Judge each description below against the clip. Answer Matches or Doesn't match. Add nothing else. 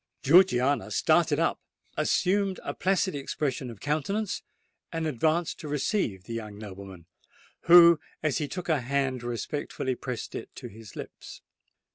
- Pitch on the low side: Doesn't match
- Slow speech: Matches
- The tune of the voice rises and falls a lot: Matches